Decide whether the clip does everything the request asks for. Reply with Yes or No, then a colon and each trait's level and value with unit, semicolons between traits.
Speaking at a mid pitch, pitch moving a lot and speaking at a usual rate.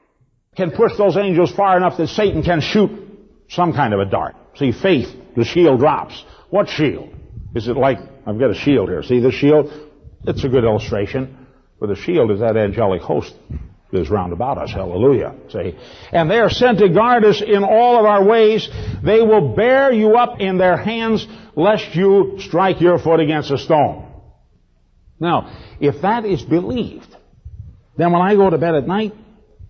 Yes: medium, 175 Hz; wide, 7.8 semitones; average, 185 wpm